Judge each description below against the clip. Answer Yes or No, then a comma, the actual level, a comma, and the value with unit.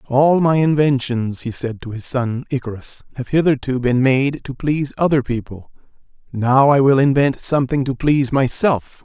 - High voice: No, low, 135 Hz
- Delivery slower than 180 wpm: Yes, average, 165 wpm